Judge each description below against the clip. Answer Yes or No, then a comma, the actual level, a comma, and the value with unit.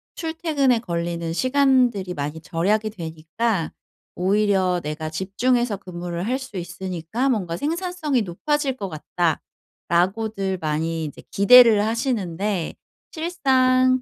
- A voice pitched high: Yes, high, 200 Hz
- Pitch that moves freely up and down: Yes, wide, 6.9 semitones